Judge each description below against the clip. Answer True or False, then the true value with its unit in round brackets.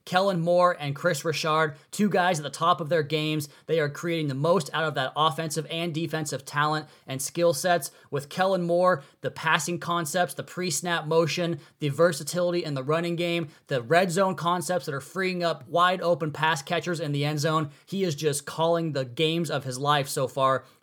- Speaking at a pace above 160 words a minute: True (205 wpm)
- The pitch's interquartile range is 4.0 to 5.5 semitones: False (2.4 semitones)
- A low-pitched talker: False (165 Hz)